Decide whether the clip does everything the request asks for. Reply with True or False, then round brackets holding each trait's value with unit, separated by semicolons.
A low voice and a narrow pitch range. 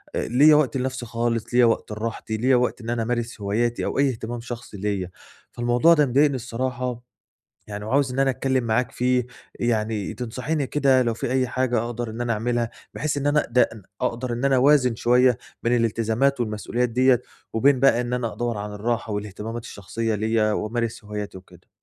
True (120 Hz; 2.3 semitones)